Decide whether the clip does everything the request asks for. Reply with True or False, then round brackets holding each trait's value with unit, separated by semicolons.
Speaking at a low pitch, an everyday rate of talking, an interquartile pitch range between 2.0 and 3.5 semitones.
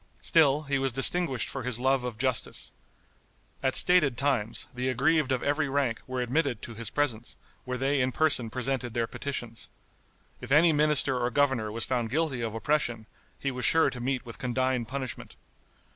True (130 Hz; 175 wpm; 2.8 semitones)